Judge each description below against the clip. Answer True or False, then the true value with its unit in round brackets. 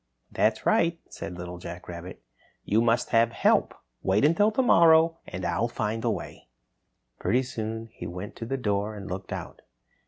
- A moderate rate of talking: True (165 wpm)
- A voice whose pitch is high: False (115 Hz)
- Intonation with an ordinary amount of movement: False (5.8 semitones)